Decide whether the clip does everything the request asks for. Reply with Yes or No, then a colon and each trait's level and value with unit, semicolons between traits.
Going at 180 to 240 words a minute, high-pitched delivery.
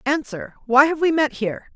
Yes: fast, 205 wpm; very high, 280 Hz